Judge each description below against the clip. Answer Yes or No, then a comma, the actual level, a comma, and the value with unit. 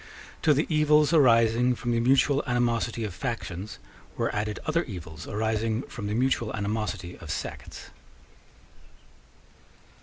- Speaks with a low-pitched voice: Yes, low, 115 Hz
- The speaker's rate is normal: No, slow, 125 wpm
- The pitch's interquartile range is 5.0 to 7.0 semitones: No, average, 3.8 semitones